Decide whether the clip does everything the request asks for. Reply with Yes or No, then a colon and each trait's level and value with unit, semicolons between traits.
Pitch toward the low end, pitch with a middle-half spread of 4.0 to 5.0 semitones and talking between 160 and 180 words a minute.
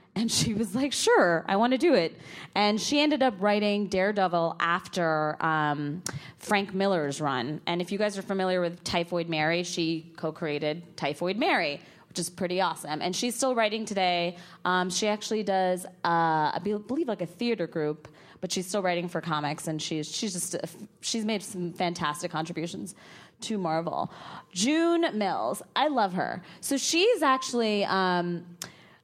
No: medium, 180 Hz; average, 4.3 semitones; average, 170 wpm